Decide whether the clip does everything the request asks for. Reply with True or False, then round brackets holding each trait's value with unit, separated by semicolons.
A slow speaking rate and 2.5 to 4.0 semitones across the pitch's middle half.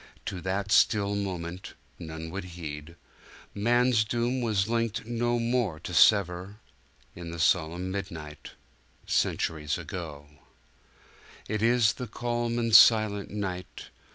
False (120 wpm; 5.4 semitones)